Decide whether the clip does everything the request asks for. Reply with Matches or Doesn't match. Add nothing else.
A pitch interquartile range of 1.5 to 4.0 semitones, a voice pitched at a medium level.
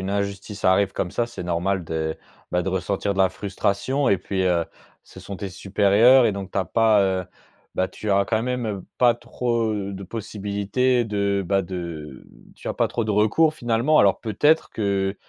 Doesn't match